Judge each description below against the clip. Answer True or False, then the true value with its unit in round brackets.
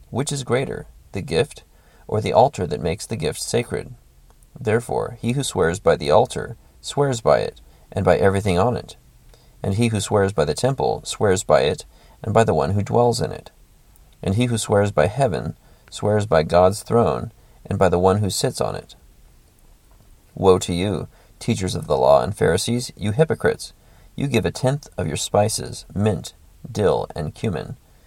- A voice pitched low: True (105 Hz)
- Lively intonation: False (3.9 semitones)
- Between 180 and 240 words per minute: True (185 wpm)